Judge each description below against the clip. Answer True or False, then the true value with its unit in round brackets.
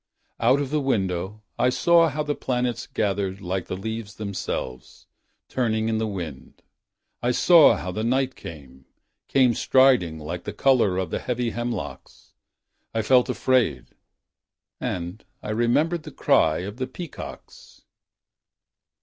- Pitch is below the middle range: True (115 Hz)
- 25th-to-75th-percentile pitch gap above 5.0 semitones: True (5.5 semitones)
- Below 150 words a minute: True (140 wpm)